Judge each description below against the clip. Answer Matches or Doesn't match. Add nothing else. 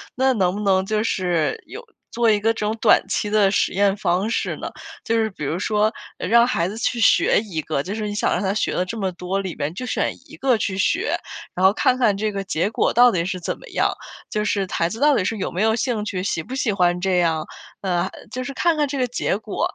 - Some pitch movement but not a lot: Matches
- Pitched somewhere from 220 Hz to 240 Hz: Doesn't match